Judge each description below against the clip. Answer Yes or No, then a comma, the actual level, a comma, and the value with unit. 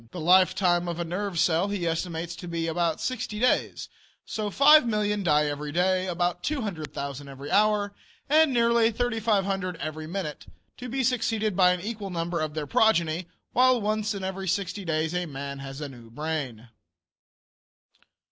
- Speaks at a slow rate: No, average, 165 wpm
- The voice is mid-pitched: Yes, medium, 180 Hz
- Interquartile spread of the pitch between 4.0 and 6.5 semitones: Yes, average, 4.9 semitones